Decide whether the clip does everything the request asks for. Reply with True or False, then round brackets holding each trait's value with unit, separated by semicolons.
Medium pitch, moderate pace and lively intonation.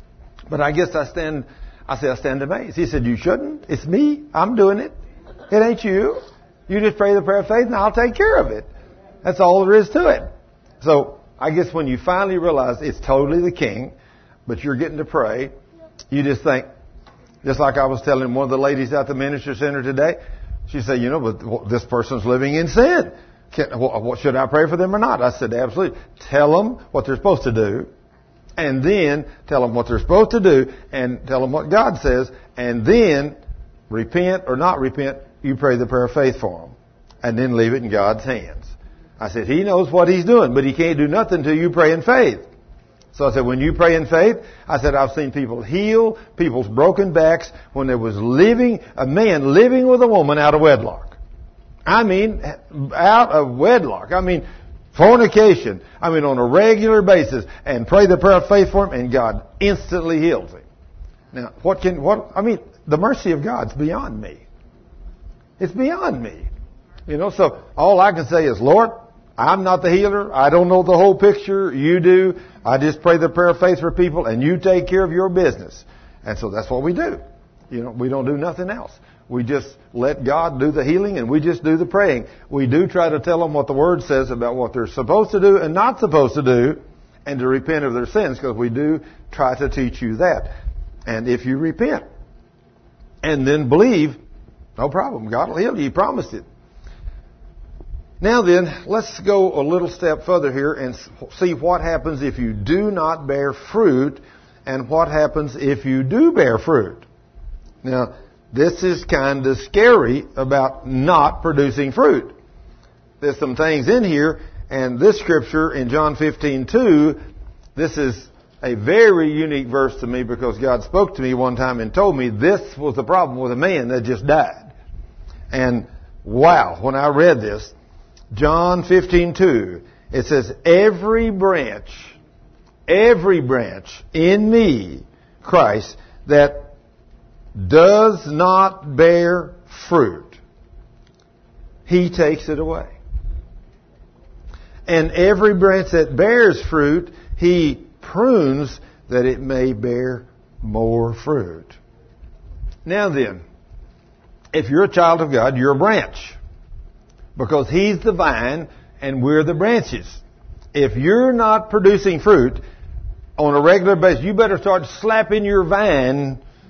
True (150 Hz; 175 wpm; 6.2 semitones)